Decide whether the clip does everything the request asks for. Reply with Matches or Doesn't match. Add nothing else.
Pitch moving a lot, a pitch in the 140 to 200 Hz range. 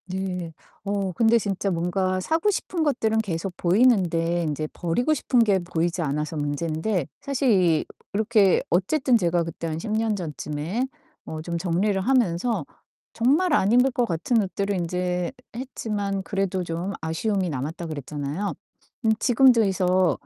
Doesn't match